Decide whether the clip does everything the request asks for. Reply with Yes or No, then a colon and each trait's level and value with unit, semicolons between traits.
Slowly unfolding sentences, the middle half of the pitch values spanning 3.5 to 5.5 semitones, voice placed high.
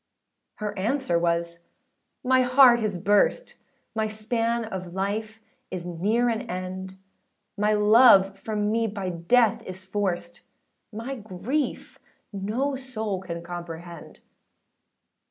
Yes: slow, 120 wpm; average, 3.8 semitones; high, 210 Hz